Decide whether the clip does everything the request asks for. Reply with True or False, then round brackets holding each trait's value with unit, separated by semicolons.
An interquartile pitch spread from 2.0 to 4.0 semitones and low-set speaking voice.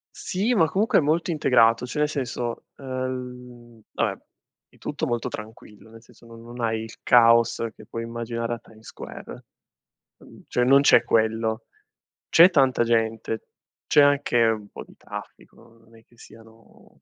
True (2.5 semitones; 120 Hz)